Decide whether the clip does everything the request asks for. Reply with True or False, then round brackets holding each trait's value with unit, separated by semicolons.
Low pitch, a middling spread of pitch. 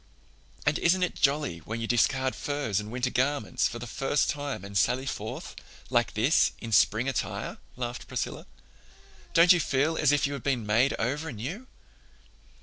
True (130 Hz; 4.2 semitones)